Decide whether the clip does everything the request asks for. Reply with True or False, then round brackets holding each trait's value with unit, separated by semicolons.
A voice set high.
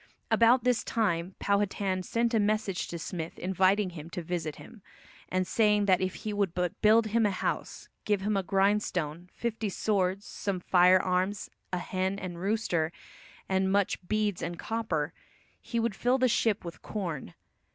True (195 Hz)